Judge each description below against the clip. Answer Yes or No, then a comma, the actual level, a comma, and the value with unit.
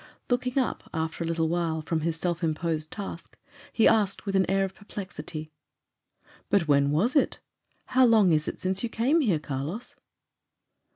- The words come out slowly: No, average, 170 wpm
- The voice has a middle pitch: Yes, medium, 175 Hz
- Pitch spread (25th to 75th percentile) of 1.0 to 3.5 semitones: No, average, 5.1 semitones